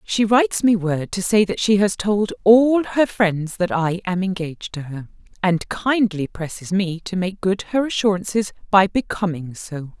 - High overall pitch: Yes, high, 195 Hz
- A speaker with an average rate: Yes, average, 185 wpm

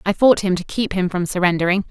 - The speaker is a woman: Yes, female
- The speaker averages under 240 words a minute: No, fast, 250 wpm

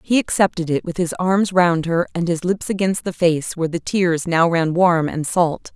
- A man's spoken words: No, female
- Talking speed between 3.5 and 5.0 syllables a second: Yes, 4.7 syllables/s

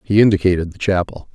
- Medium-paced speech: Yes, average, 180 wpm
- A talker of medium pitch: No, very low, 95 Hz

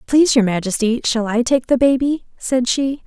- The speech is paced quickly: No, average, 195 wpm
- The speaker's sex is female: Yes, female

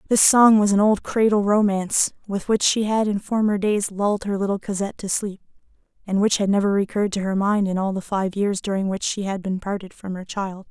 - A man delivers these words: No, female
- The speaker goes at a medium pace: No, fast, 235 wpm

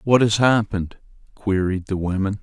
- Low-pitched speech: Yes, low, 100 Hz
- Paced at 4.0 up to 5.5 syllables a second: Yes, 5.0 syllables/s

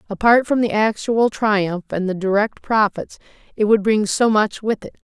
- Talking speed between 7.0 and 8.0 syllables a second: No, 4.7 syllables/s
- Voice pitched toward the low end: No, high, 210 Hz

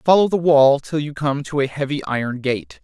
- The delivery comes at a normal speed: No, fast, 235 wpm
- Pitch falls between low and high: Yes, medium, 145 Hz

